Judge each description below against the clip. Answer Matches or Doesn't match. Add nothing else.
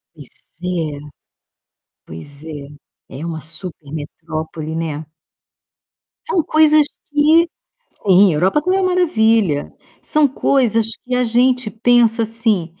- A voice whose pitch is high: Matches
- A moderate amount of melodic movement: Doesn't match